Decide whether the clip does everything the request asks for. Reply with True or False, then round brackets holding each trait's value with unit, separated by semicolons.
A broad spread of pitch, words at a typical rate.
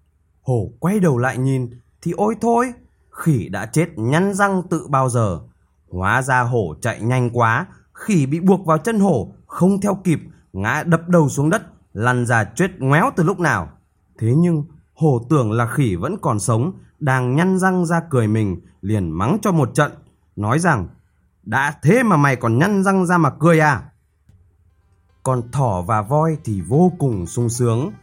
True (7.0 semitones; 180 wpm)